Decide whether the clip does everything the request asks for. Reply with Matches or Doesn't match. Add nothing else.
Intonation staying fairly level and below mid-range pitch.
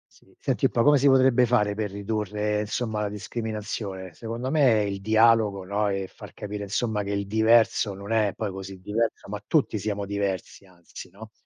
Matches